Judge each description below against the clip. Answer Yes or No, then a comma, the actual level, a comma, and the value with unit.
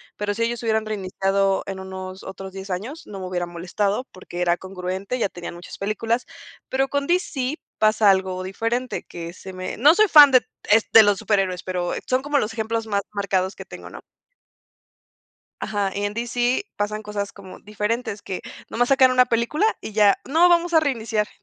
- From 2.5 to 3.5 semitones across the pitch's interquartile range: No, average, 4.3 semitones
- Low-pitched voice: No, high, 210 Hz